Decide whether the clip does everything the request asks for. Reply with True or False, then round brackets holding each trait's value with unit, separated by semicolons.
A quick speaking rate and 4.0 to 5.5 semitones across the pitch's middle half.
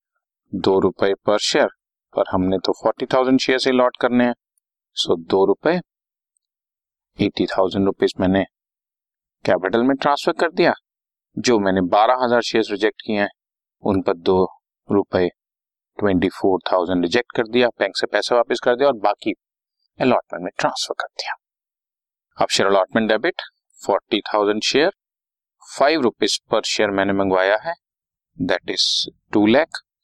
False (150 wpm; 4.5 semitones)